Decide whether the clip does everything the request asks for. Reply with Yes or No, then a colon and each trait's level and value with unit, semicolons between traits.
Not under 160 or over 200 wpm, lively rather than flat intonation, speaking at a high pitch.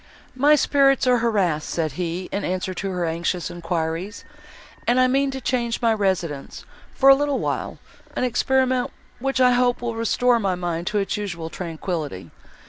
Yes: average, 170 wpm; wide, 6.4 semitones; high, 205 Hz